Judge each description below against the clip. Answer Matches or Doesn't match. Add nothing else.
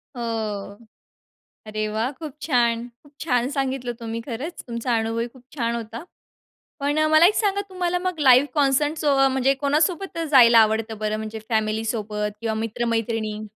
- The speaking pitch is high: Matches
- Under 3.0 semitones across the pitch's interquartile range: Doesn't match